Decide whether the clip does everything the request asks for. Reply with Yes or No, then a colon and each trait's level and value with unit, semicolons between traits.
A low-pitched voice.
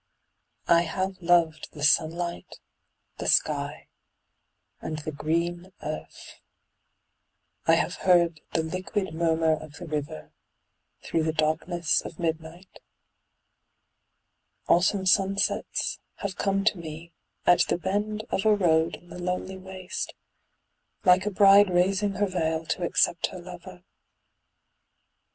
No: medium, 175 Hz